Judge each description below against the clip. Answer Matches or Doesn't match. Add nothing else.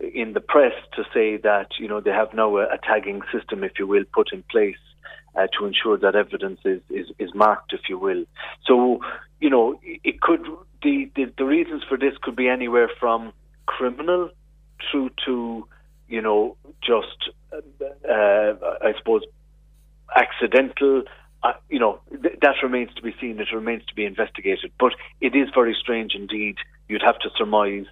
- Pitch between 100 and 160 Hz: Matches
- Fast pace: Doesn't match